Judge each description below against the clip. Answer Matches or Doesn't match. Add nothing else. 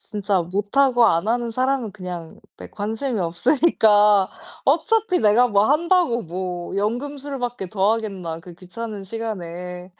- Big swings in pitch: Doesn't match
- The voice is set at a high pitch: Matches